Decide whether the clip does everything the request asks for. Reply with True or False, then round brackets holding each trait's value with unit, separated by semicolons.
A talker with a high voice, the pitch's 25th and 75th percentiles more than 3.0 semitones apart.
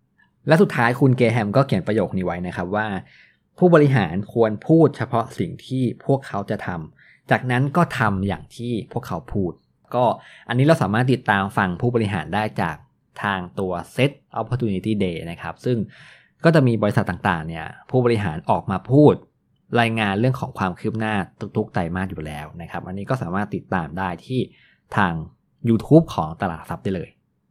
False (110 Hz; 5.1 semitones)